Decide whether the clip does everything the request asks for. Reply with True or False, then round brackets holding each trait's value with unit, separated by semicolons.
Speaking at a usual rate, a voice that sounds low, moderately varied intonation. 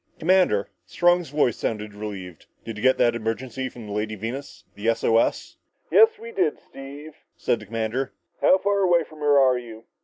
False (190 wpm; 125 Hz; 6.3 semitones)